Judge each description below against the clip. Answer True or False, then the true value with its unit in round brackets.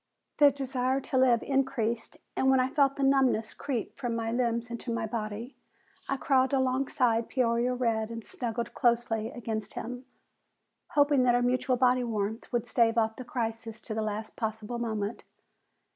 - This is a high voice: True (240 Hz)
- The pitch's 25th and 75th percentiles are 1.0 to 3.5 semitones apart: True (2.5 semitones)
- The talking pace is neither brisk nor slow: True (165 wpm)